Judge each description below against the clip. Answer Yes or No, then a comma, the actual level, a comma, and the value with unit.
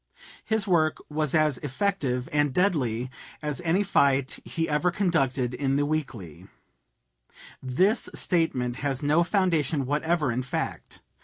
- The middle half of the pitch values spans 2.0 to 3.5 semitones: No, average, 4.3 semitones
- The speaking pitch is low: No, medium, 150 Hz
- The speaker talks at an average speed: No, slow, 130 wpm